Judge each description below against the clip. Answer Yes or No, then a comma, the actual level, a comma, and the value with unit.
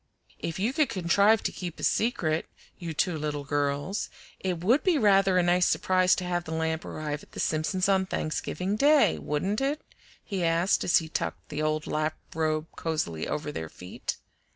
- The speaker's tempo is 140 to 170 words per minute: No, average, 185 wpm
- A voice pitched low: No, medium, 170 Hz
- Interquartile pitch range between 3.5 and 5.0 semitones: Yes, average, 3.9 semitones